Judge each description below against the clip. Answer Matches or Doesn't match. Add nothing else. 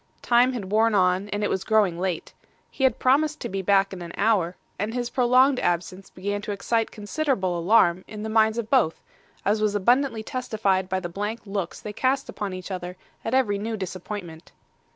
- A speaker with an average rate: Matches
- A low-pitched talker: Doesn't match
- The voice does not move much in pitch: Doesn't match